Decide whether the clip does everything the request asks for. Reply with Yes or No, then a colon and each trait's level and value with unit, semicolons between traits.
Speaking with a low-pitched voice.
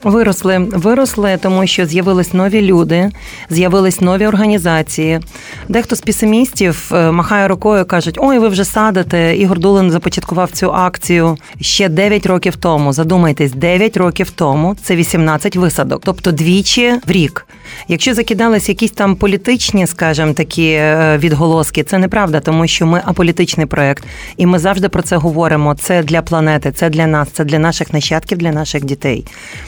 No: medium, 180 Hz